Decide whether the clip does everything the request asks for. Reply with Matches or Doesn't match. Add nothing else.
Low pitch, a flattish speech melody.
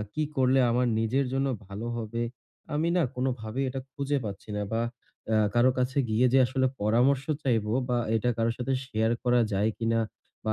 Doesn't match